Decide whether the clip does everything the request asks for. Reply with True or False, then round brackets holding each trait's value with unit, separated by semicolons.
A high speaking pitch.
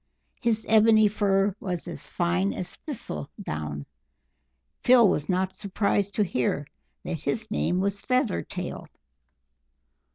True (195 Hz)